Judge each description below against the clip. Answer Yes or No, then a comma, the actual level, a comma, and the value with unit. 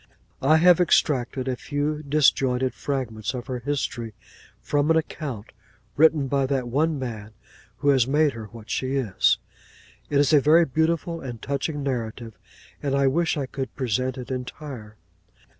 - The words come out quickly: No, average, 160 wpm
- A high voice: No, low, 135 Hz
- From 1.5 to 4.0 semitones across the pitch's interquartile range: Yes, average, 3.1 semitones